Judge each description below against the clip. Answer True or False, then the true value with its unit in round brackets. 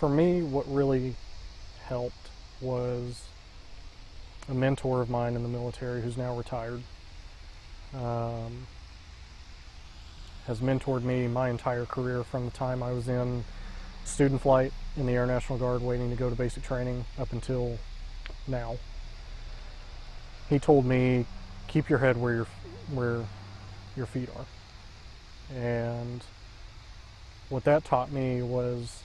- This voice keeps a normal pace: False (130 wpm)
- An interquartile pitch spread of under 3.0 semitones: False (4.7 semitones)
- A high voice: False (120 Hz)